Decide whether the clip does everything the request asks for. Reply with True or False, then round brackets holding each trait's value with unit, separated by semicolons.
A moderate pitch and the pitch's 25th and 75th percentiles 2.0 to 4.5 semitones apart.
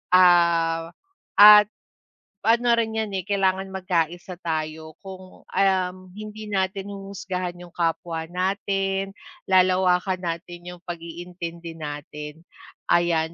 True (180 Hz; 2.5 semitones)